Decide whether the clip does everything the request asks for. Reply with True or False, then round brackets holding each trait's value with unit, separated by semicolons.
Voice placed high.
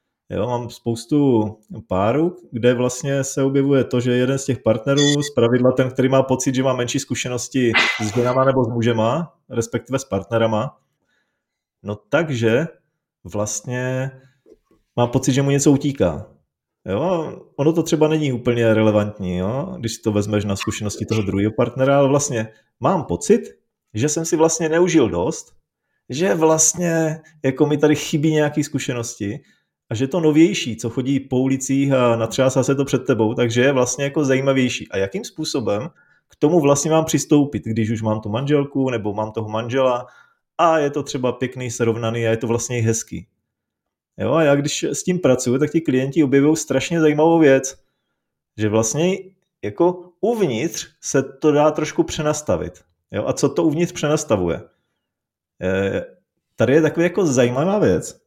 False (130 Hz)